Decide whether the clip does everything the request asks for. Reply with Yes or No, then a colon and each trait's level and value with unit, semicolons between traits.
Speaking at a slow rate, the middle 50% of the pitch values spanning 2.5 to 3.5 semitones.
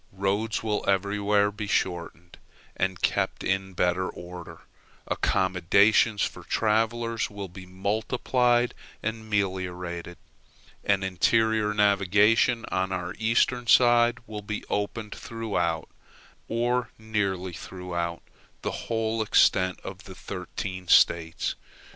Yes: slow, 105 wpm; average, 3.2 semitones